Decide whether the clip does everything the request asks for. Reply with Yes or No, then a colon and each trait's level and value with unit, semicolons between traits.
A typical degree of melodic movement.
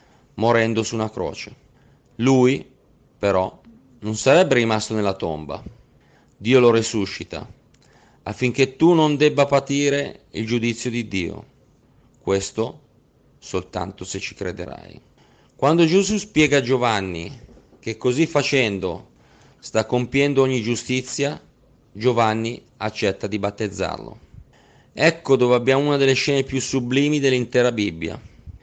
Yes: average, 4.3 semitones